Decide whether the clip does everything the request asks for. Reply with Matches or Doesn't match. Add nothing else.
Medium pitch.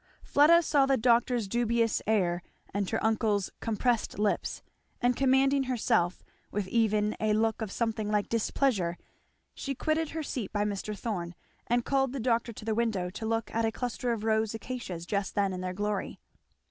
Doesn't match